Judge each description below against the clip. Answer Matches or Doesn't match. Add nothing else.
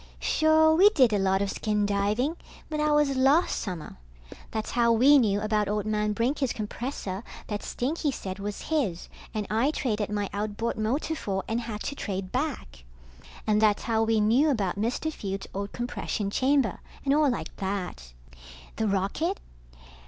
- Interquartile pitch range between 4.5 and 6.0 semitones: Matches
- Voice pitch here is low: Doesn't match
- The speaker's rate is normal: Matches